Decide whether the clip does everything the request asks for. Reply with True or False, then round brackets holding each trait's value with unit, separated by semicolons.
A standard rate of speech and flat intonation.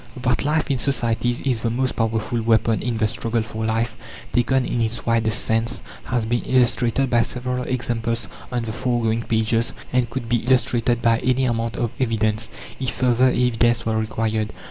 True (175 wpm; 1.8 semitones)